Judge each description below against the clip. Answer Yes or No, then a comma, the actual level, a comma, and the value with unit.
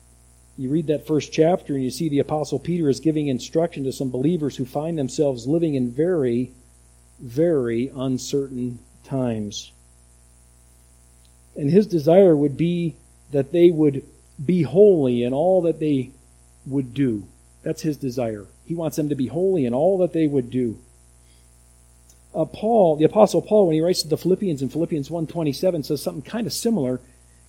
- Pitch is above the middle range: No, medium, 140 Hz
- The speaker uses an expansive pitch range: Yes, wide, 7.4 semitones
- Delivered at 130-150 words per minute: No, average, 165 wpm